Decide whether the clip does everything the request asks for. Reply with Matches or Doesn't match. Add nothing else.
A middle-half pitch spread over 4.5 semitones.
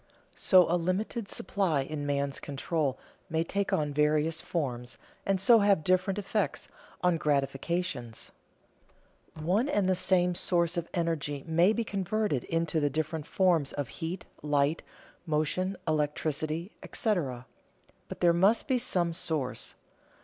Doesn't match